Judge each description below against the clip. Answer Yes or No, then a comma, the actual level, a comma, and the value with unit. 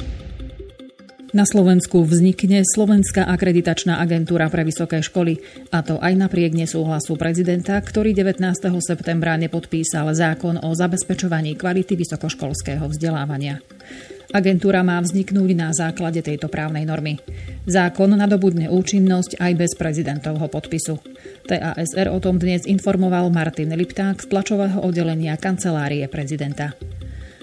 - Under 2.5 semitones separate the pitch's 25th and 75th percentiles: No, average, 2.8 semitones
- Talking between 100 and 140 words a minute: Yes, average, 115 wpm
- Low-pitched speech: No, medium, 170 Hz